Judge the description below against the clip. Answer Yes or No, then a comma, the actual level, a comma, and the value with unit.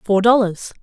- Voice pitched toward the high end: Yes, high, 210 Hz